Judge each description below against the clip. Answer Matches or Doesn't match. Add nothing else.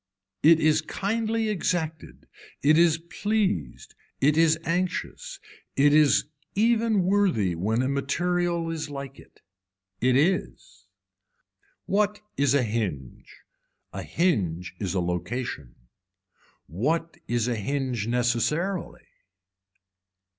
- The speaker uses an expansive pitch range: Matches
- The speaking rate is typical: Doesn't match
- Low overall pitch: Doesn't match